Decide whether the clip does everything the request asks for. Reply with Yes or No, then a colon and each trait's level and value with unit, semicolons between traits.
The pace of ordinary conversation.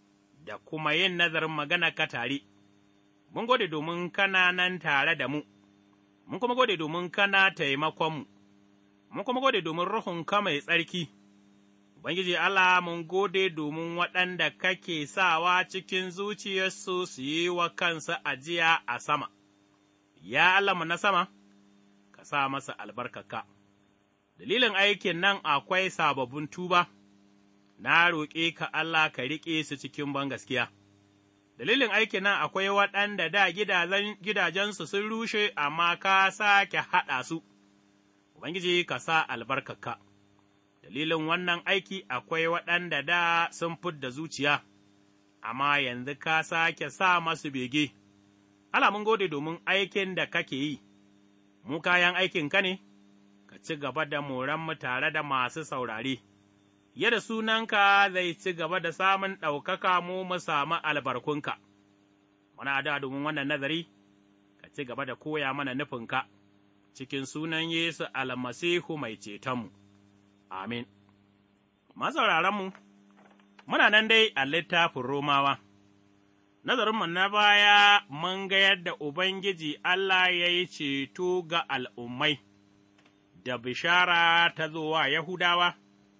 No: slow, 120 wpm